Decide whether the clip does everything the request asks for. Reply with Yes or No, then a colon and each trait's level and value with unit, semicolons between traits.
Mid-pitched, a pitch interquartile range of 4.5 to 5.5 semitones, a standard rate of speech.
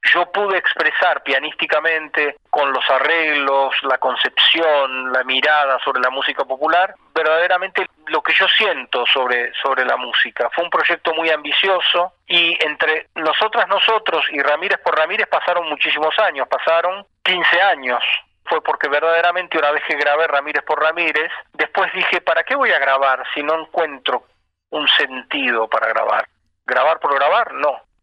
No: medium, 155 Hz; average, 3.4 semitones; average, 150 wpm